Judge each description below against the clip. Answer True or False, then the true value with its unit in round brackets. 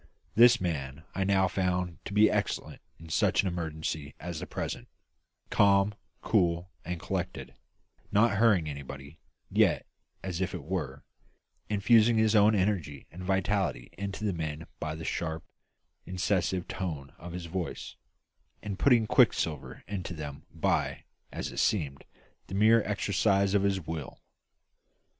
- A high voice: False (90 Hz)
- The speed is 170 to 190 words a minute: False (140 wpm)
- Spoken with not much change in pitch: False (4.0 semitones)